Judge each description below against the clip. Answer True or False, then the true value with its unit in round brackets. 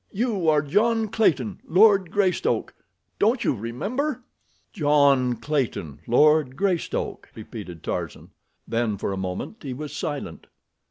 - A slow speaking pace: True (115 wpm)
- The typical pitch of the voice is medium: True (150 Hz)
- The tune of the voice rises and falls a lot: True (9.0 semitones)